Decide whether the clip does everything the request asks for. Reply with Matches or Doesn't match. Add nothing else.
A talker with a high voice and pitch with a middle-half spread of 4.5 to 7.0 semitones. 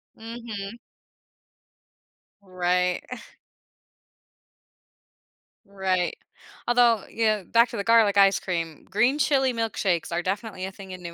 Doesn't match